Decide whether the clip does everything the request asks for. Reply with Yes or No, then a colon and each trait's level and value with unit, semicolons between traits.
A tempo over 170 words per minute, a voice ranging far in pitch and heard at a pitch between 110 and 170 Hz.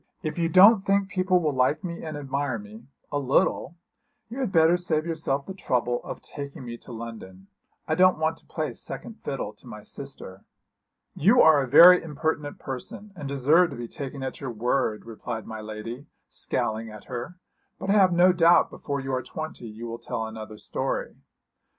Yes: average, 190 wpm; wide, 6.3 semitones; medium, 140 Hz